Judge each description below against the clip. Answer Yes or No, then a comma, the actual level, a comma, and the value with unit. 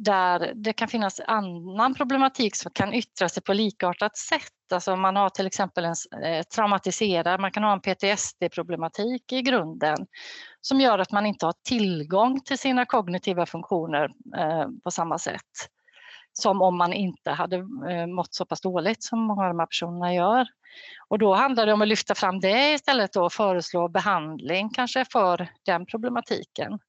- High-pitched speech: Yes, high, 195 Hz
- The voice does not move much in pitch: No, average, 4.8 semitones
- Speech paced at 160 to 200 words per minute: Yes, average, 165 wpm